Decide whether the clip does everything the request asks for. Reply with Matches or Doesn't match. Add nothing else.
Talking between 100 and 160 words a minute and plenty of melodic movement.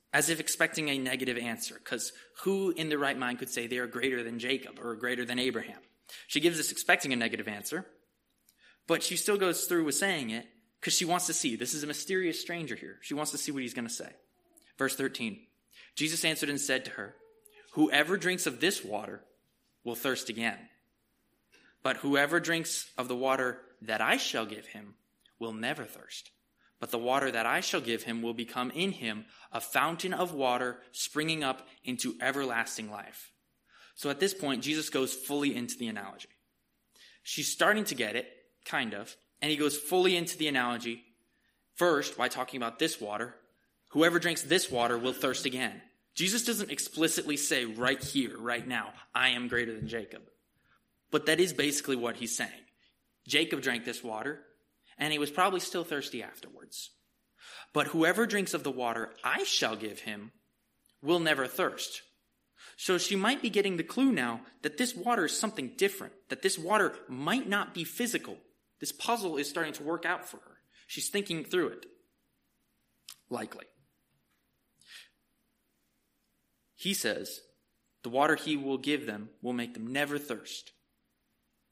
Doesn't match